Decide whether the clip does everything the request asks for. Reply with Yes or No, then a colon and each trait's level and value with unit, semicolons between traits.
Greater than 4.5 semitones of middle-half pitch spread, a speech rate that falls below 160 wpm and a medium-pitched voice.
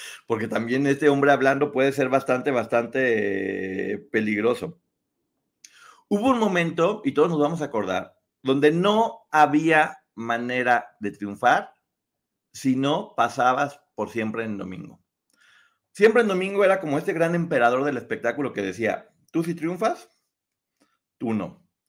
Yes: average, 5.2 semitones; average, 145 wpm; medium, 145 Hz